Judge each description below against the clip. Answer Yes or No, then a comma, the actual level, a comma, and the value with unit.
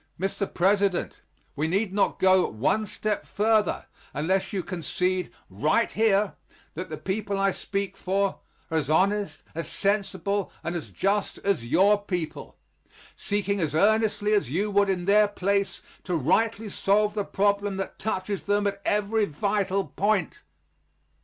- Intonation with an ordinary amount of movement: No, narrow, 2.1 semitones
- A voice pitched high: Yes, high, 200 Hz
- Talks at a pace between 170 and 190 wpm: No, average, 145 wpm